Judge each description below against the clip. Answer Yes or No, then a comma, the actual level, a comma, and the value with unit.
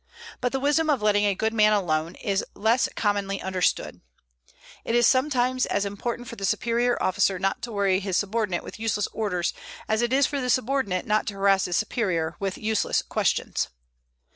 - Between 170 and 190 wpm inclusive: Yes, average, 185 wpm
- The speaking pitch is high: Yes, high, 210 Hz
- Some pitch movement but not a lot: Yes, average, 3.6 semitones